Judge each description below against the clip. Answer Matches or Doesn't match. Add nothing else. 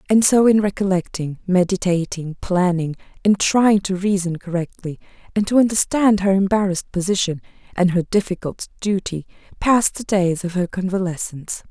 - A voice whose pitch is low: Doesn't match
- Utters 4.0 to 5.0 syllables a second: Doesn't match